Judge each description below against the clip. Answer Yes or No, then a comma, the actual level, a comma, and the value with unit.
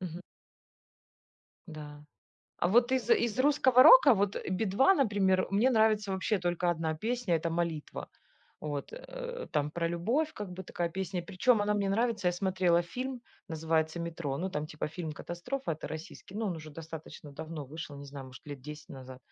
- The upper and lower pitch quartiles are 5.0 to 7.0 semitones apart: Yes, wide, 5.5 semitones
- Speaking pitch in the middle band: Yes, medium, 175 Hz